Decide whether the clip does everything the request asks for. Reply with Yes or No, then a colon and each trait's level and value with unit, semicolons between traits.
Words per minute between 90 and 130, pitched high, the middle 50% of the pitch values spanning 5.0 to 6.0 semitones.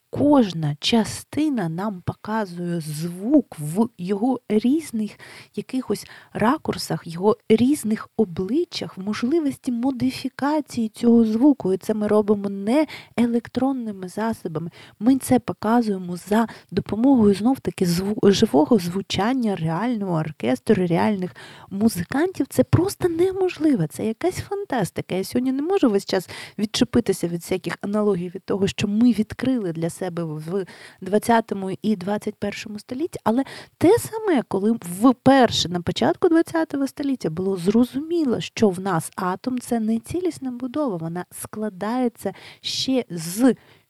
Yes: average, 125 wpm; high, 215 Hz; wide, 5.6 semitones